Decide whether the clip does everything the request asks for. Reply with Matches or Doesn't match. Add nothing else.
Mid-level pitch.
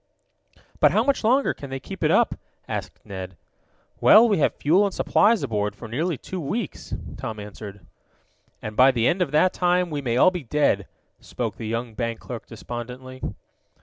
Doesn't match